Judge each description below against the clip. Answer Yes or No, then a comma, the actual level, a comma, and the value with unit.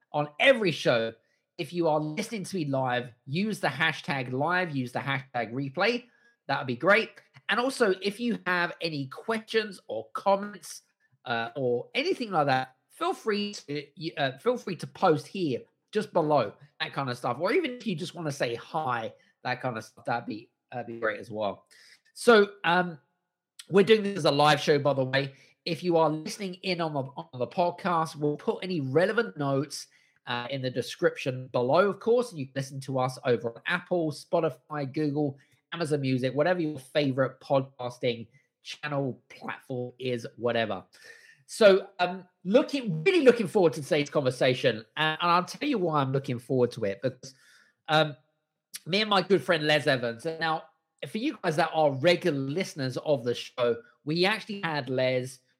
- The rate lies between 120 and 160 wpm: No, average, 180 wpm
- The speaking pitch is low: No, medium, 155 Hz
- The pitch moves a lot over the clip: Yes, wide, 5.7 semitones